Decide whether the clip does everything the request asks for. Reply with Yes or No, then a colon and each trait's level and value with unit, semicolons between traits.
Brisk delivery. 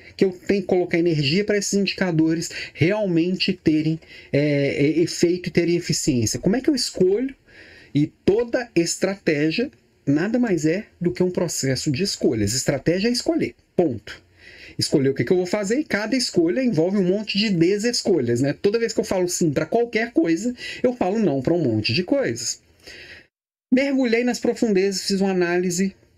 No: average, 175 wpm